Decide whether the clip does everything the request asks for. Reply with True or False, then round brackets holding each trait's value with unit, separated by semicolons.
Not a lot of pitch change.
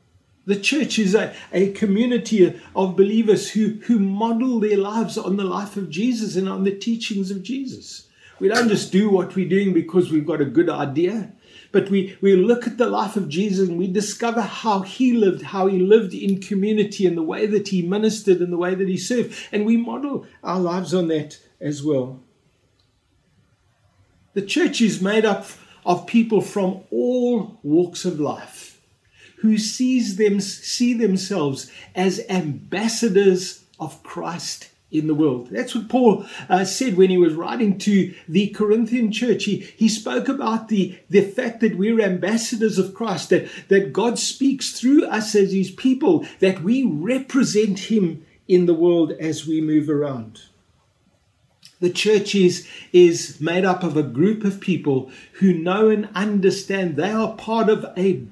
False (3.6 semitones)